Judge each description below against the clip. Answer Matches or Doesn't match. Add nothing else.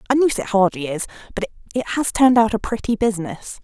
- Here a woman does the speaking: Matches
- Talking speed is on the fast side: Matches